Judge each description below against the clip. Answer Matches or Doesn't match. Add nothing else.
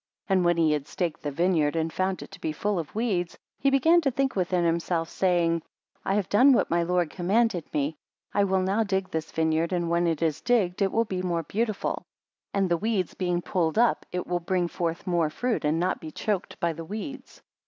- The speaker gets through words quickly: Matches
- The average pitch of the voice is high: Doesn't match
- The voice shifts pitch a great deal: Doesn't match